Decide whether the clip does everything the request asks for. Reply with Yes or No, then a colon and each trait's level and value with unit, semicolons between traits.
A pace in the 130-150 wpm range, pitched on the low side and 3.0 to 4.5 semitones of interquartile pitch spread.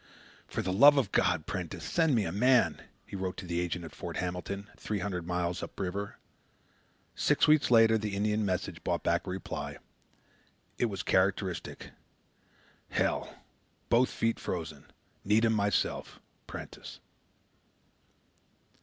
Yes: average, 140 wpm; low, 100 Hz; average, 3.7 semitones